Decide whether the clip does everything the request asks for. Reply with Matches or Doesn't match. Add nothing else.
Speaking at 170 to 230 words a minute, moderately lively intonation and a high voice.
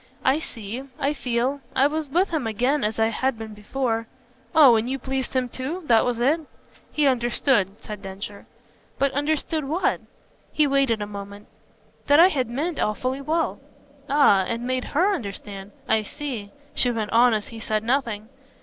Matches